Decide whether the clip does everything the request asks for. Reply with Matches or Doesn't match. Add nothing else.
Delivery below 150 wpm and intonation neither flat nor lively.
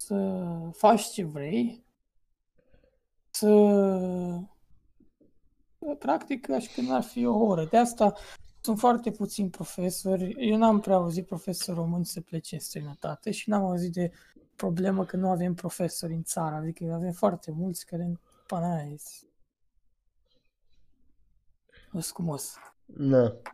Matches